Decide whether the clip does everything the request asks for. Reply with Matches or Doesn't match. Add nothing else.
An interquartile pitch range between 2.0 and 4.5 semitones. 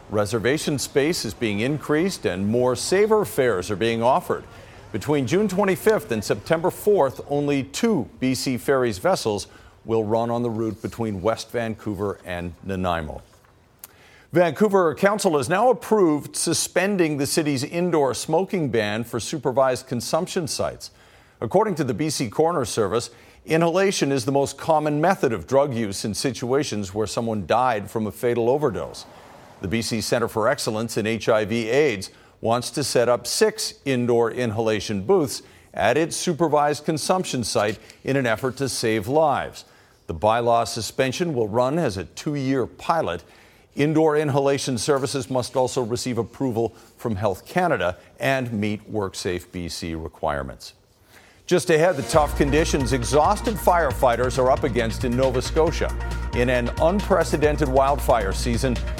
Doesn't match